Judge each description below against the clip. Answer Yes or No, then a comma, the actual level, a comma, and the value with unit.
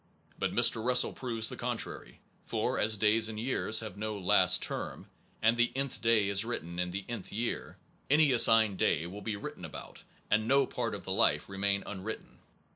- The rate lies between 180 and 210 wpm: Yes, average, 190 wpm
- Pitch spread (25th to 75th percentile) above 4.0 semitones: No, average, 2.7 semitones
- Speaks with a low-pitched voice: Yes, low, 110 Hz